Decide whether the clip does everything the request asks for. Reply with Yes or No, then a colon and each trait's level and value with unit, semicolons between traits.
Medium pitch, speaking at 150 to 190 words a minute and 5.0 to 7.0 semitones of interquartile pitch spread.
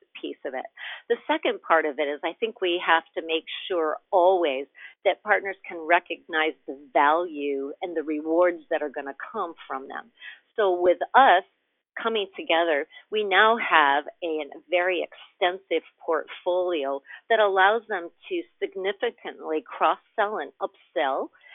Yes: medium, 180 Hz; average, 155 wpm; wide, 5.4 semitones